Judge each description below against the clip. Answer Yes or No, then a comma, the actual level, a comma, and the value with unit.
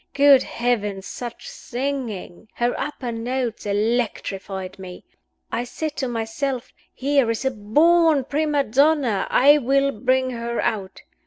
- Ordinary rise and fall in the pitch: Yes, average, 4.0 semitones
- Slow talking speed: Yes, slow, 130 wpm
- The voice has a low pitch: No, high, 245 Hz